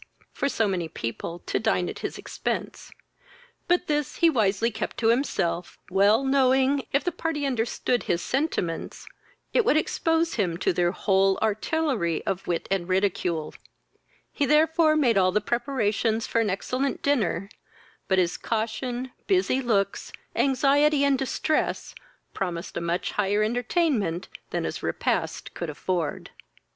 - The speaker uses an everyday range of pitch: No, wide, 6.7 semitones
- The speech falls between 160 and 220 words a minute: No, average, 145 wpm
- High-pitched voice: Yes, high, 230 Hz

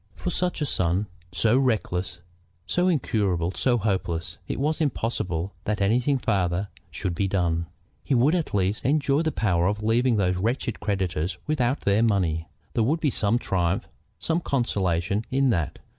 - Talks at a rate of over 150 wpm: Yes, average, 160 wpm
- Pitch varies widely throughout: Yes, wide, 6.2 semitones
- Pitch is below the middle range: Yes, low, 105 Hz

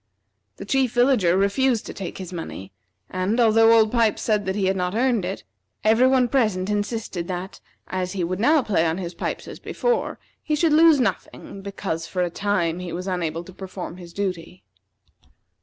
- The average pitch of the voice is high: Yes, high, 195 Hz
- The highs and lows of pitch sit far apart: No, average, 4.1 semitones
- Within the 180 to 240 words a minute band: Yes, average, 190 wpm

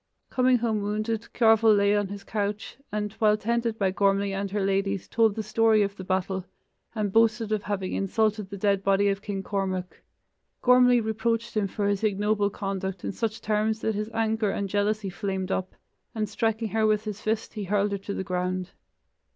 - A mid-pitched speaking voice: No, high, 210 Hz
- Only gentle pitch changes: Yes, narrow, 1.9 semitones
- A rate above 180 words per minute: Yes, average, 190 wpm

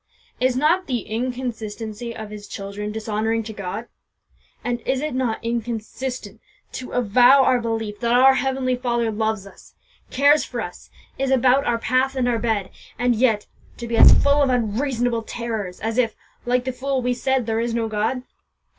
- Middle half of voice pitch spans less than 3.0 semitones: Yes, narrow, 2.6 semitones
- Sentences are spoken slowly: No, average, 175 wpm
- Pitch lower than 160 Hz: No, high, 235 Hz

